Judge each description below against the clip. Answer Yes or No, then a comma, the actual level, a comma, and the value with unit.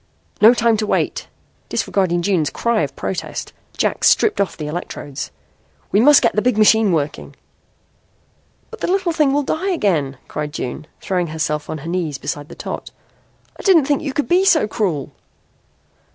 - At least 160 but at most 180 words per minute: Yes, average, 170 wpm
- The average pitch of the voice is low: No, high, 205 Hz